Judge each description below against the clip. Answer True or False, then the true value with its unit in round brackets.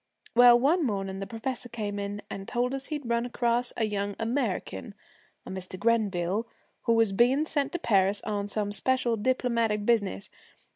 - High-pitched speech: True (225 Hz)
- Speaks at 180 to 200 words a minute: False (165 wpm)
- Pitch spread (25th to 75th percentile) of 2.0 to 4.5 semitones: True (3.4 semitones)